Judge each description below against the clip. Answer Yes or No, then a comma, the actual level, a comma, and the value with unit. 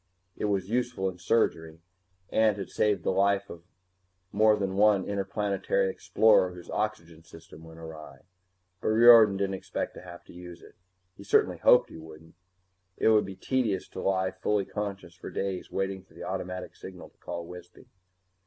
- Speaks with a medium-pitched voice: No, very low, 95 Hz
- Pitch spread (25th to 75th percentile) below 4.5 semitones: Yes, average, 2.9 semitones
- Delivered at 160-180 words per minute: Yes, average, 170 wpm